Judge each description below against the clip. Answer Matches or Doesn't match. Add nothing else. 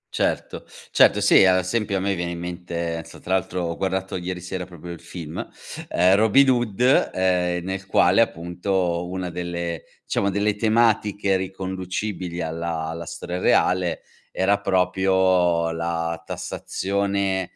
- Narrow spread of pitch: Matches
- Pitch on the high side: Doesn't match